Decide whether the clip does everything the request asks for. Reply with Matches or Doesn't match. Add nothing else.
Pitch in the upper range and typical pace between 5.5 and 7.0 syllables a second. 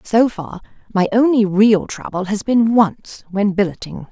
Doesn't match